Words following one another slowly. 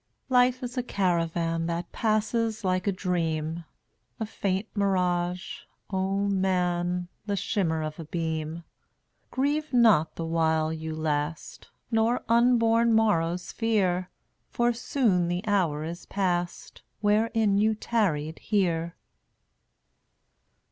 Yes: slow, 120 wpm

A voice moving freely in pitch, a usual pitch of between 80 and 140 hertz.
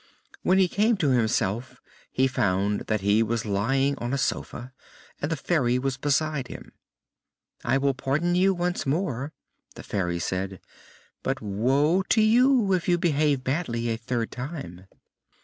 Yes: wide, 6.4 semitones; low, 135 Hz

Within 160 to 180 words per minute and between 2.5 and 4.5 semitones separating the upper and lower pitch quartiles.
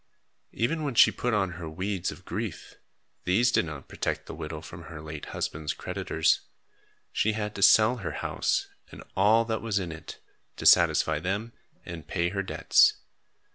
No: average, 175 wpm; average, 5.2 semitones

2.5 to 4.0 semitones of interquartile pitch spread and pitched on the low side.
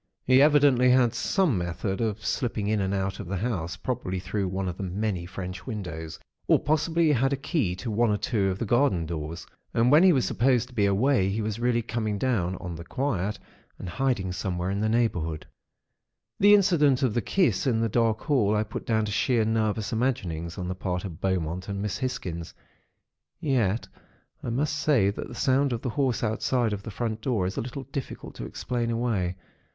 No: average, 5.1 semitones; low, 110 Hz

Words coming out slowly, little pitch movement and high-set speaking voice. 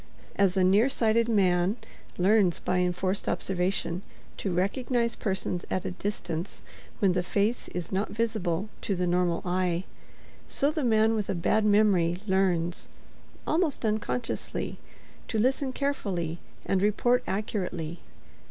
No: slow, 130 wpm; average, 3.6 semitones; high, 195 Hz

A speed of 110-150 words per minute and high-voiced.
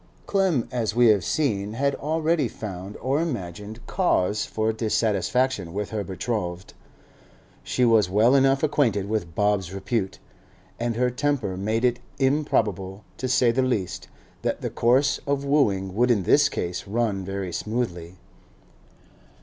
No: average, 140 wpm; low, 110 Hz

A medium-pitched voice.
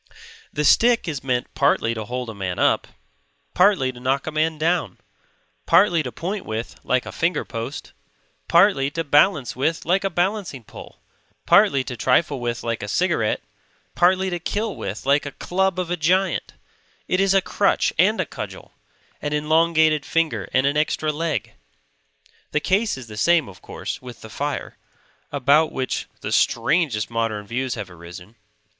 Yes: medium, 150 Hz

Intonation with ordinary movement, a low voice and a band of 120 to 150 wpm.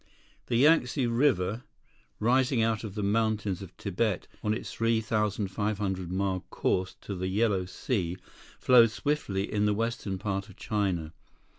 Yes: average, 3.1 semitones; low, 105 Hz; average, 140 wpm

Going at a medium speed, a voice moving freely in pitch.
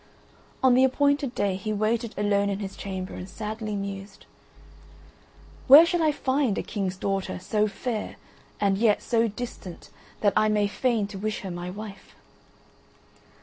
No: average, 155 wpm; average, 3.1 semitones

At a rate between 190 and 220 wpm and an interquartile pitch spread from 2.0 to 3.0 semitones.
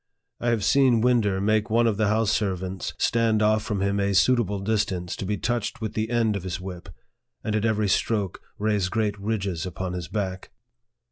Yes: average, 195 wpm; narrow, 2.6 semitones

